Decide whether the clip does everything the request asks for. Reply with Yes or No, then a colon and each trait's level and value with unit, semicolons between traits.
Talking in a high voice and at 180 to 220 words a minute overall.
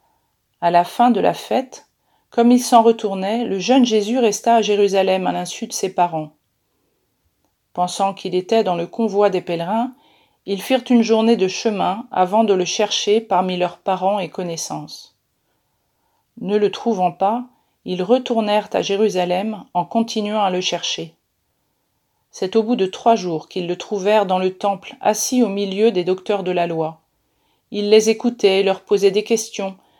No: high, 200 Hz; average, 170 wpm